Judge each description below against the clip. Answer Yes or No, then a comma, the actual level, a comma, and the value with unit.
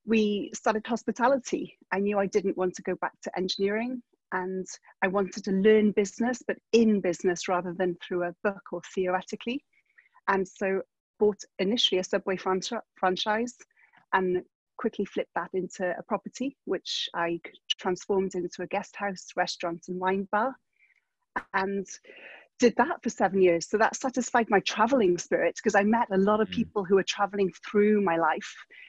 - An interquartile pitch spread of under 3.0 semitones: No, average, 3.7 semitones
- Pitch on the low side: No, high, 200 Hz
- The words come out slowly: No, average, 165 wpm